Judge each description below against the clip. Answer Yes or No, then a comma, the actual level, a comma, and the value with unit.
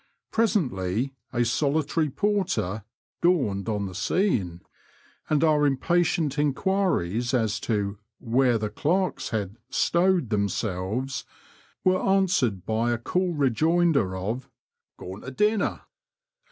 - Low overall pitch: Yes, low, 130 Hz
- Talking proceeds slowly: Yes, slow, 110 wpm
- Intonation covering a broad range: Yes, wide, 8.4 semitones